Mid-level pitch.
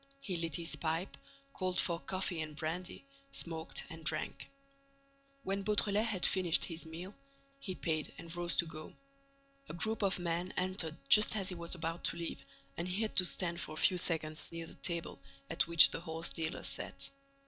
Yes: medium, 170 Hz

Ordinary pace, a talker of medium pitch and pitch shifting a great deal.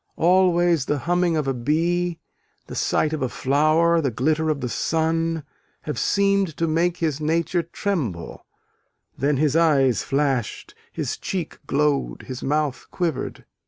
No: average, 145 wpm; medium, 155 Hz; average, 3.4 semitones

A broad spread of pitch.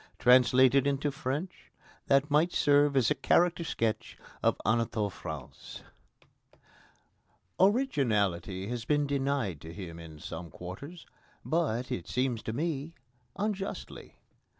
Yes: wide, 6.1 semitones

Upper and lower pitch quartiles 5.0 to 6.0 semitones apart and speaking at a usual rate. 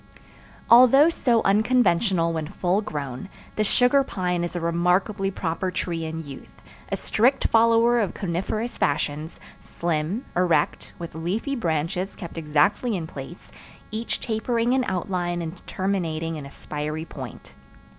No: average, 5.3 semitones; slow, 130 wpm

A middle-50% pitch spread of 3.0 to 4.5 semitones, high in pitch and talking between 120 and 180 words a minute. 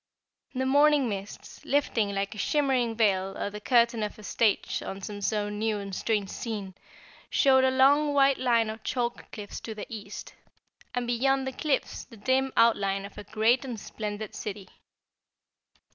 Yes: average, 4.1 semitones; high, 225 Hz; average, 165 wpm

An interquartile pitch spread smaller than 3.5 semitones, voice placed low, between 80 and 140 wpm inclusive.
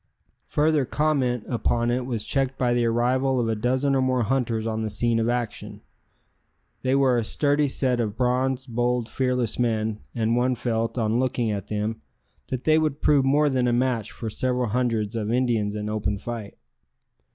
No: narrow, 2.5 semitones; low, 120 Hz; average, 185 wpm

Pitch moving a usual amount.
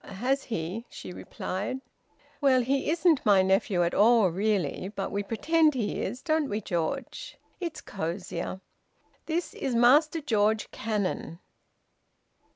No: wide, 6.2 semitones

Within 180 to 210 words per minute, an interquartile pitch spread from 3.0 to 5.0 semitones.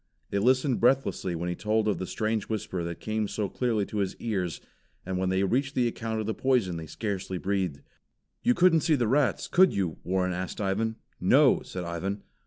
Yes: average, 200 wpm; average, 4.2 semitones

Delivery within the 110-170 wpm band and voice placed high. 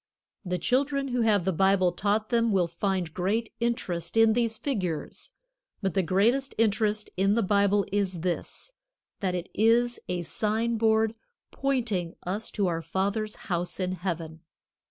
Yes: average, 155 wpm; high, 200 Hz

